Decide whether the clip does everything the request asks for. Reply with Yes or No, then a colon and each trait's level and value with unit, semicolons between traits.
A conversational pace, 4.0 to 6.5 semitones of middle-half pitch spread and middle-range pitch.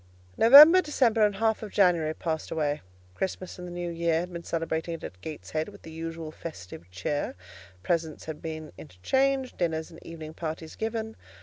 Yes: average, 170 wpm; average, 4.5 semitones; medium, 165 Hz